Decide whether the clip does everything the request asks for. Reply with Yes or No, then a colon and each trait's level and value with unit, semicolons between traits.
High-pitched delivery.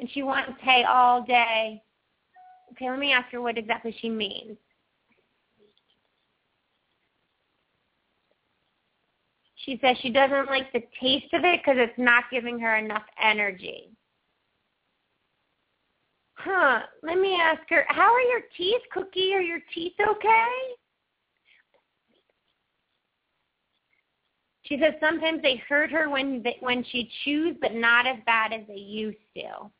Yes: very high, 265 Hz